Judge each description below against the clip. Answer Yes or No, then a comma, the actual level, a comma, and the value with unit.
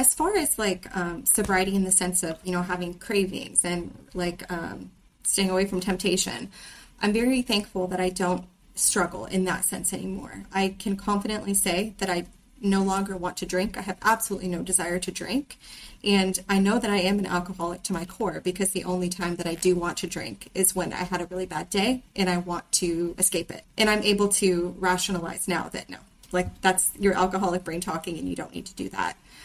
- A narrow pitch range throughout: Yes, narrow, 1.8 semitones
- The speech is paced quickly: Yes, fast, 215 wpm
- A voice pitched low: No, medium, 185 Hz